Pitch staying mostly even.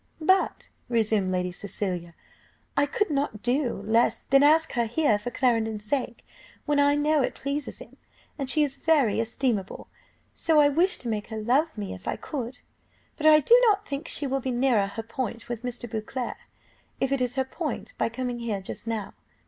No: average, 4.6 semitones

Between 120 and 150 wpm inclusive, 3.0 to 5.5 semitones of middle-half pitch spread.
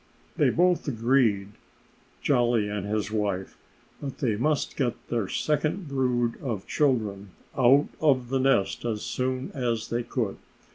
Yes: average, 140 wpm; average, 4.0 semitones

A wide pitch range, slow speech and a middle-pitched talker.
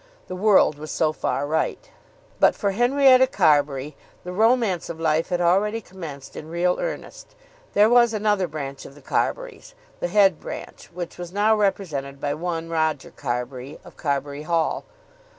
No: wide, 5.8 semitones; average, 160 wpm; medium, 175 Hz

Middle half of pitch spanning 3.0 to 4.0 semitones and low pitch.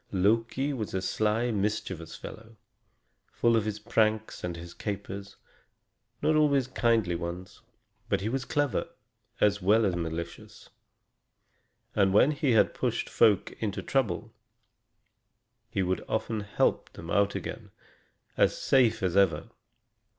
Yes: average, 3.4 semitones; low, 105 Hz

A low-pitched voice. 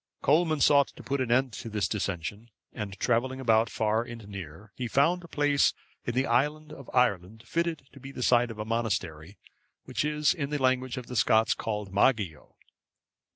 Yes: low, 120 Hz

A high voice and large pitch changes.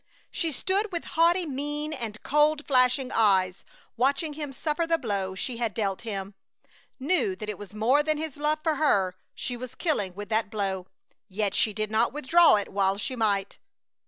Yes: very high, 250 Hz; wide, 6.7 semitones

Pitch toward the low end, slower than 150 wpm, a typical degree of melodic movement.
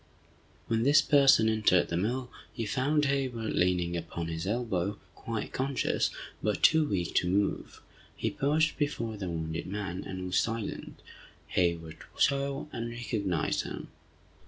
No: low, 110 Hz; average, 140 wpm; wide, 6.4 semitones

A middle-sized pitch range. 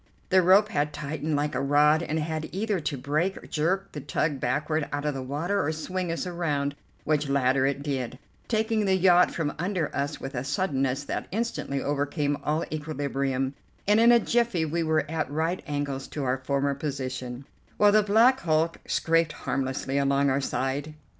Yes: average, 3.7 semitones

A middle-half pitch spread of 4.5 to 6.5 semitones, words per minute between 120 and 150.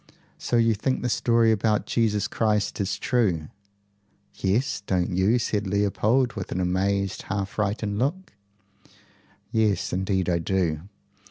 No: average, 3.1 semitones; slow, 135 wpm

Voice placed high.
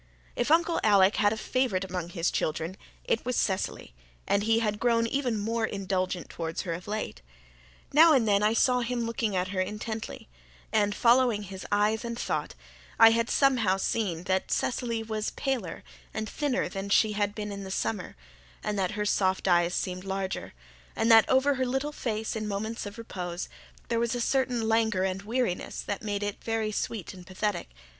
Yes: high, 215 Hz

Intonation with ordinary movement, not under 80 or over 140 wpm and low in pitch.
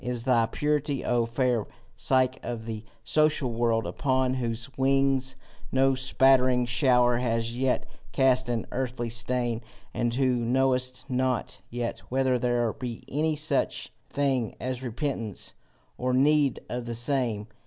No: narrow, 1.9 semitones; slow, 135 wpm; low, 125 Hz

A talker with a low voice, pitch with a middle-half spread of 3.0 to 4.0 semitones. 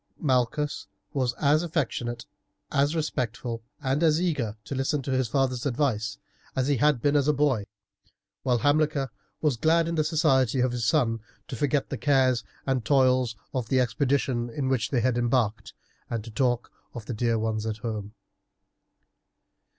Yes: low, 130 Hz; average, 3.7 semitones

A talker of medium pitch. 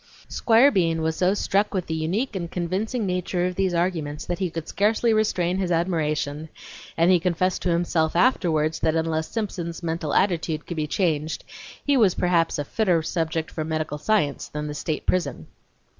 Yes: medium, 170 Hz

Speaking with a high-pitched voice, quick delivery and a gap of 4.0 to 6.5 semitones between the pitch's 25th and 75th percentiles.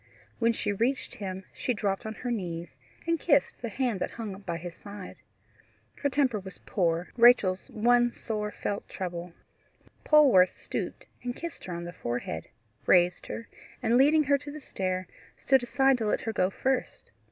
No: high, 215 Hz; average, 175 wpm; average, 5.3 semitones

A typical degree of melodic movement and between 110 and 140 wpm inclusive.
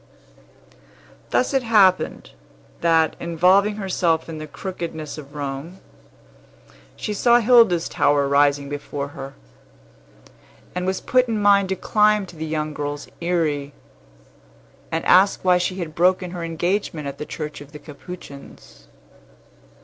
Yes: average, 4.5 semitones; slow, 135 wpm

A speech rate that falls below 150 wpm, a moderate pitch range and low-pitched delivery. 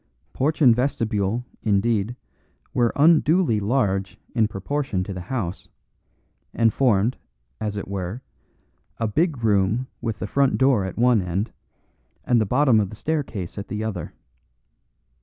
Yes: average, 140 wpm; average, 4.5 semitones; low, 110 Hz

